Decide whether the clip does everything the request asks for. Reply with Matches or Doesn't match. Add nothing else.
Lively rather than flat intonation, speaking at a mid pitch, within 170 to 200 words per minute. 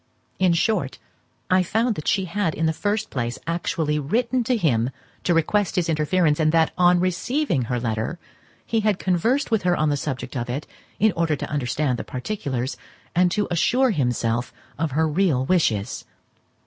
Matches